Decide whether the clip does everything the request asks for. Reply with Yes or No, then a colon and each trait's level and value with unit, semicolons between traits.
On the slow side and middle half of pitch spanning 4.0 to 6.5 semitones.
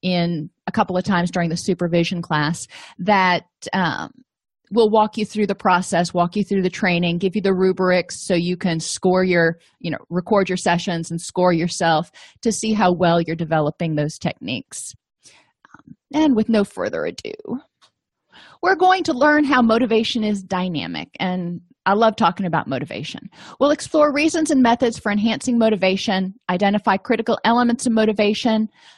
No: average, 165 wpm; average, 4.4 semitones